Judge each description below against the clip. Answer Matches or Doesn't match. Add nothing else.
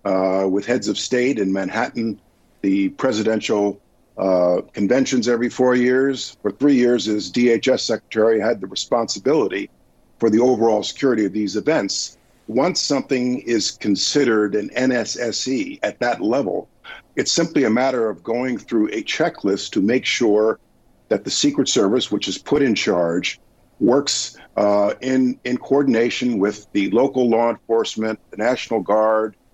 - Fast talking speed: Doesn't match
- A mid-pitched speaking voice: Doesn't match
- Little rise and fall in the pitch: Doesn't match